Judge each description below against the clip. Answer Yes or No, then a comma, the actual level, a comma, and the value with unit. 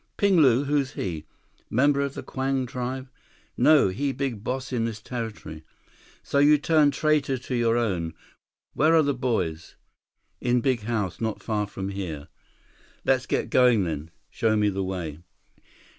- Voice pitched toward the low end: Yes, low, 120 Hz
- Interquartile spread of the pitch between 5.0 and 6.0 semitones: Yes, wide, 5.4 semitones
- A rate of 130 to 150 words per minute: No, average, 160 wpm